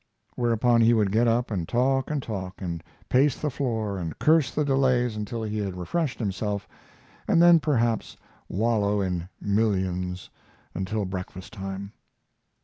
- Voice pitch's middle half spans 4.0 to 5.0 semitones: Yes, average, 4.4 semitones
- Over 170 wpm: No, average, 145 wpm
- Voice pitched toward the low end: Yes, low, 110 Hz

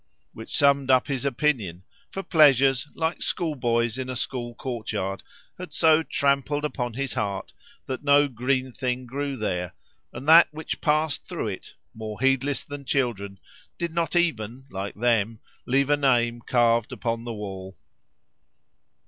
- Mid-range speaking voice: No, low, 130 Hz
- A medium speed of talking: Yes, average, 150 wpm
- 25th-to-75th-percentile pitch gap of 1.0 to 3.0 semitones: No, average, 3.8 semitones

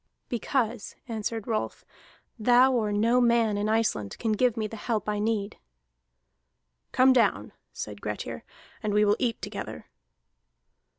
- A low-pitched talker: No, high, 225 Hz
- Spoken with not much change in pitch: Yes, narrow, 2.2 semitones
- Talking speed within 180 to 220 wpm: No, slow, 135 wpm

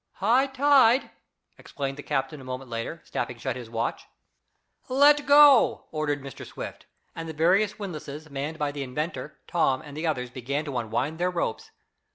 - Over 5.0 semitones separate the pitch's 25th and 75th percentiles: Yes, wide, 5.5 semitones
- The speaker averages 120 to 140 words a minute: No, average, 170 wpm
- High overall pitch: No, medium, 150 Hz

